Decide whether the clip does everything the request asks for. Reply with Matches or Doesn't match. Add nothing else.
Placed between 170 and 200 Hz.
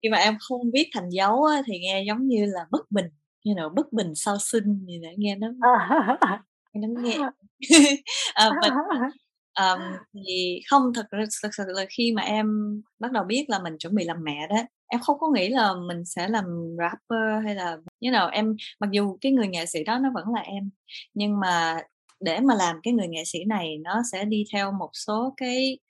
Doesn't match